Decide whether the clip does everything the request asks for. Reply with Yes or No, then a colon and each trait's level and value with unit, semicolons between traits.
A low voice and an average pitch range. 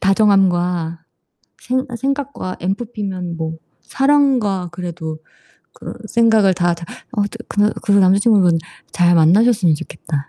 No: high, 195 Hz; average, 4.3 semitones